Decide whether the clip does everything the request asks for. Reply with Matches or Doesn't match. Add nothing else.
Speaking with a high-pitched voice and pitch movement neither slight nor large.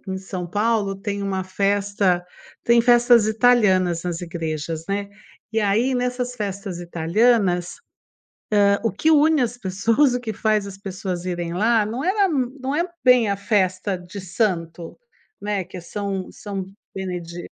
Matches